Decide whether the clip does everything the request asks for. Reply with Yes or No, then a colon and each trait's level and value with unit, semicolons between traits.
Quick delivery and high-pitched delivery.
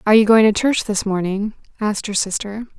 Yes: fast, 215 wpm; high, 210 Hz